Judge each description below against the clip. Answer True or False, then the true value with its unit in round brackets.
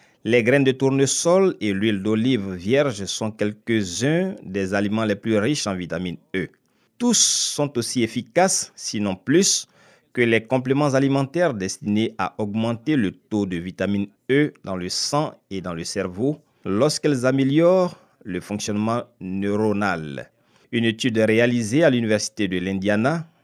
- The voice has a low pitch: True (115 Hz)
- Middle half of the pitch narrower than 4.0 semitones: False (5.3 semitones)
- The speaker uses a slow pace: True (140 wpm)